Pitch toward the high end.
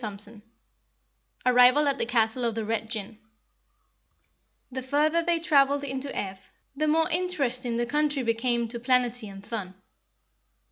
Yes: very high, 250 Hz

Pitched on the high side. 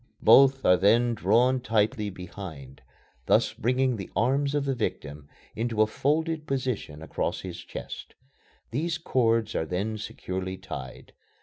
No: low, 110 Hz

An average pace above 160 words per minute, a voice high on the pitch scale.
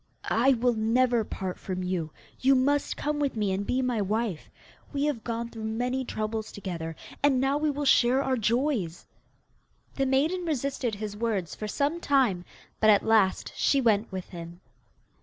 Yes: average, 175 wpm; high, 230 Hz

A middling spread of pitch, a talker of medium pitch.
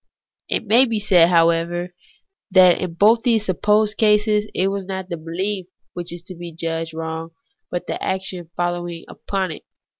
Yes: average, 3.4 semitones; medium, 180 Hz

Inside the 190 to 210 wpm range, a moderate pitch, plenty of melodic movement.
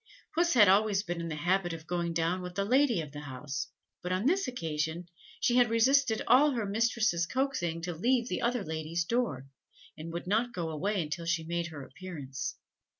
Yes: average, 200 wpm; medium, 180 Hz; wide, 6.1 semitones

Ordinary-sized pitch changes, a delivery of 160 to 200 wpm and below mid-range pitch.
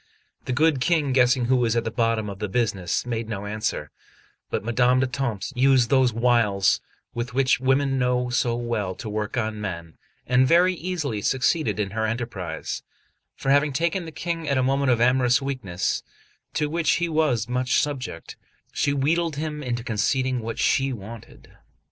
Yes: average, 3.6 semitones; average, 170 wpm; low, 125 Hz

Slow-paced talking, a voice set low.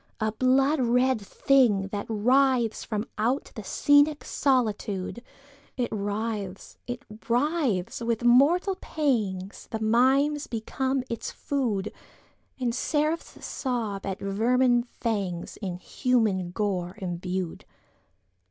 No: slow, 85 wpm; high, 235 Hz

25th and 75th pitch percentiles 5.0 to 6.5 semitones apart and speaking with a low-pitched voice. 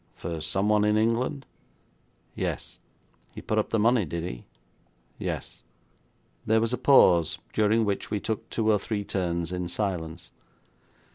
No: average, 4.1 semitones; low, 105 Hz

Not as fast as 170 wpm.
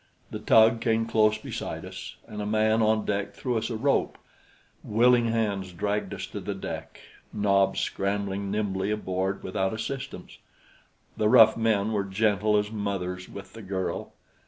Yes: average, 160 wpm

